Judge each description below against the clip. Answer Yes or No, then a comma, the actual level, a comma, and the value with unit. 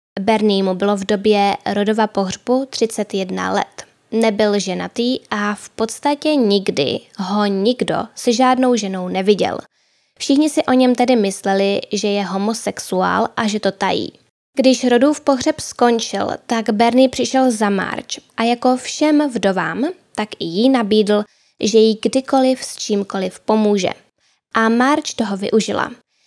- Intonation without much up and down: No, average, 3.8 semitones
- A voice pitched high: Yes, high, 225 Hz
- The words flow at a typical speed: Yes, average, 140 wpm